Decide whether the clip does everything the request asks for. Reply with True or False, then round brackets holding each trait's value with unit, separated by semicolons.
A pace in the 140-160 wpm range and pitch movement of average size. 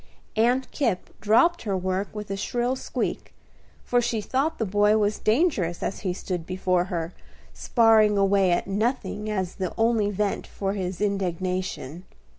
True (155 wpm; 3.2 semitones)